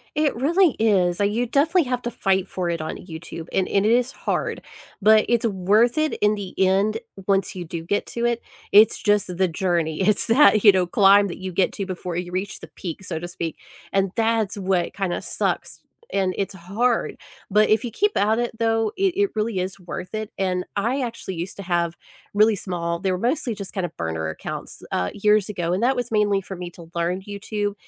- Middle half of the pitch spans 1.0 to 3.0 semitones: No, average, 3.7 semitones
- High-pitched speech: Yes, high, 200 Hz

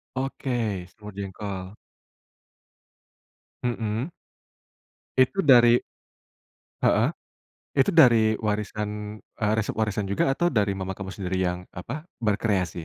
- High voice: No, low, 105 Hz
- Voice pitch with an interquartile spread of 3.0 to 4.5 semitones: Yes, average, 3.6 semitones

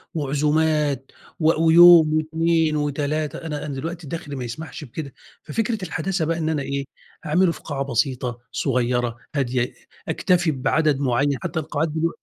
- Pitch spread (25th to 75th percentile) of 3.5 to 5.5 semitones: No, average, 2.9 semitones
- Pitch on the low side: No, medium, 150 Hz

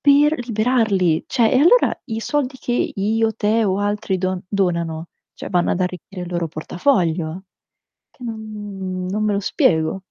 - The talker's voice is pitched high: Yes, high, 200 Hz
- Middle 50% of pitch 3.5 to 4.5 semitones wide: Yes, average, 3.9 semitones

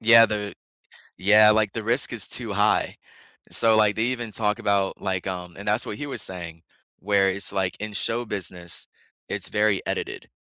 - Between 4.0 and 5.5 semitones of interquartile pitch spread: No, narrow, 2.5 semitones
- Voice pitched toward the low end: Yes, low, 105 Hz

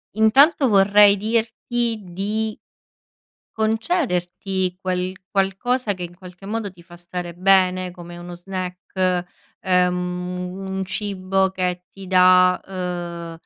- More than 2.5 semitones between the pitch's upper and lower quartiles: No, narrow, 2.2 semitones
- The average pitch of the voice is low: No, medium, 185 Hz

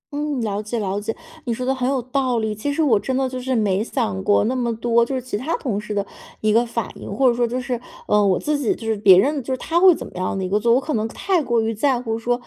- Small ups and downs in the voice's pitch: No, average, 3.6 semitones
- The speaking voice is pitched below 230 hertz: No, high, 235 Hz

